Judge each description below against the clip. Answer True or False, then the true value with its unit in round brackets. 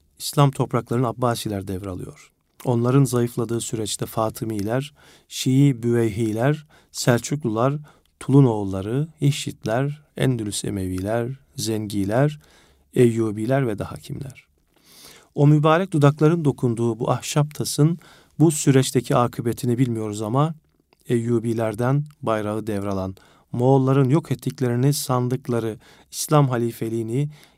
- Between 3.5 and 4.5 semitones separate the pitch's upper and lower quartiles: True (3.8 semitones)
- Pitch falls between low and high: False (125 Hz)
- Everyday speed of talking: False (85 wpm)